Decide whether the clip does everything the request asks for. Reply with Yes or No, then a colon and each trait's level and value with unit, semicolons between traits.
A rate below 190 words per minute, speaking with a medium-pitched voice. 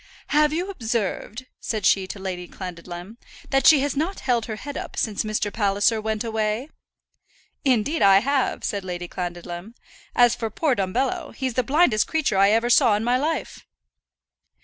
No: average, 170 wpm; high, 225 Hz